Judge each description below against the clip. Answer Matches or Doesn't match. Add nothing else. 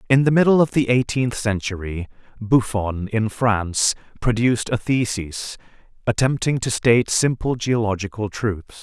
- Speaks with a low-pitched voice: Matches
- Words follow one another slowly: Matches